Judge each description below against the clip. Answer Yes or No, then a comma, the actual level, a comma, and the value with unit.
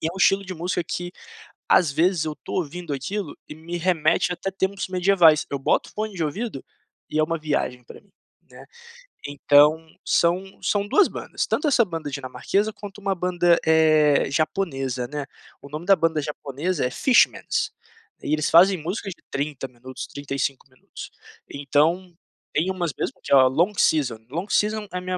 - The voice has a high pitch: No, medium, 165 Hz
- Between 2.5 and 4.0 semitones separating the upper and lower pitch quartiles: No, average, 4.4 semitones